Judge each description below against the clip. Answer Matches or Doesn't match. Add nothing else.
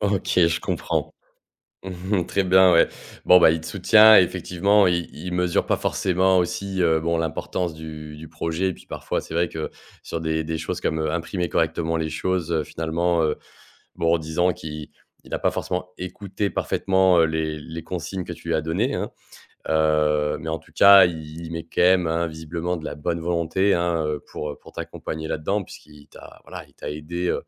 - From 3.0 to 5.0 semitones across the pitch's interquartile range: Doesn't match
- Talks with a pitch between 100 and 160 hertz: Doesn't match